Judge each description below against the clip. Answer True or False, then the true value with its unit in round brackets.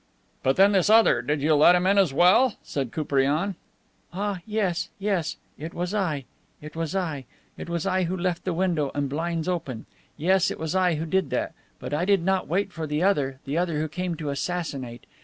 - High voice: False (170 Hz)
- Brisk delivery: True (210 wpm)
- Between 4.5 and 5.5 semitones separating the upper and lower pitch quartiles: False (3.9 semitones)